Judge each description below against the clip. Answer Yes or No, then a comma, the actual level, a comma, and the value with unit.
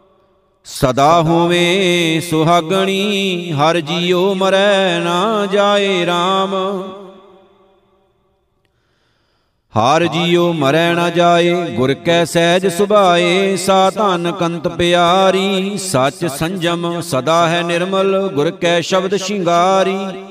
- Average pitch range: No, narrow, 2.0 semitones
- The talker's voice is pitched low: No, medium, 175 Hz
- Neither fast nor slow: No, slow, 90 wpm